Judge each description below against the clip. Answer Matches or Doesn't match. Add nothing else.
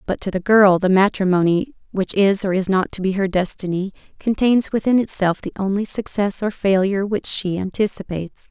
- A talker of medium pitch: Doesn't match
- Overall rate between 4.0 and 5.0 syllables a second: Doesn't match